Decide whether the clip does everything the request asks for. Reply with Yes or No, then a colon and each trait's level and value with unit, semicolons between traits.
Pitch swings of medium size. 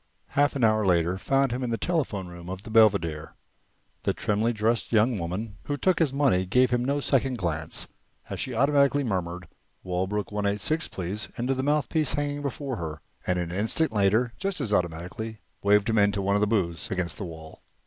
No: wide, 6.3 semitones